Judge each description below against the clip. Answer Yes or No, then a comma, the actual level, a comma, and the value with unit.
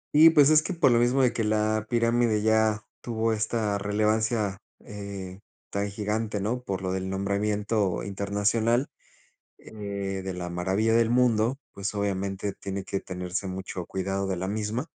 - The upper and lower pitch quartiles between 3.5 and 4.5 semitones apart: No, narrow, 2.5 semitones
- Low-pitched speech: Yes, low, 105 Hz